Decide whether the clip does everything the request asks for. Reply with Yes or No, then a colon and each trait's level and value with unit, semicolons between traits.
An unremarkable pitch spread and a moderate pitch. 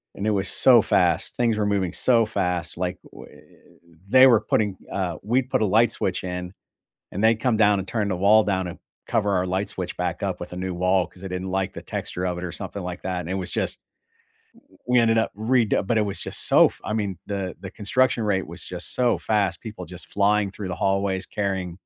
No: average, 3.0 semitones; low, 100 Hz